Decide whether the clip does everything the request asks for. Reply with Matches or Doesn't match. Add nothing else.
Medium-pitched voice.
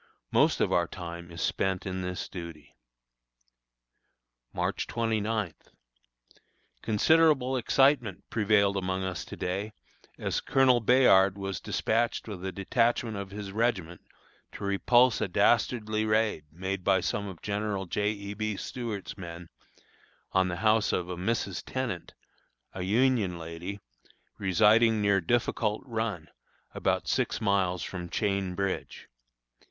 Doesn't match